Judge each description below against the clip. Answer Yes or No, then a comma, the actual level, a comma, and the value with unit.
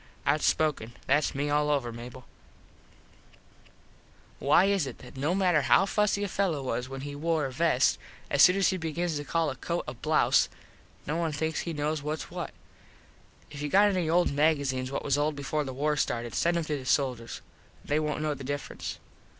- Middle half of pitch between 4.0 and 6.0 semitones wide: No, average, 3.2 semitones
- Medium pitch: Yes, medium, 150 Hz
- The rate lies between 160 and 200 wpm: Yes, average, 195 wpm